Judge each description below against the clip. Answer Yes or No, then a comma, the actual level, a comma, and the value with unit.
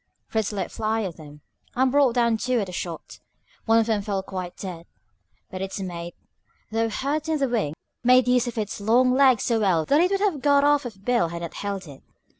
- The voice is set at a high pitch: Yes, high, 225 Hz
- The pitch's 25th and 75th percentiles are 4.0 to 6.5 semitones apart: Yes, average, 5.1 semitones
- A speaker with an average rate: No, fast, 225 wpm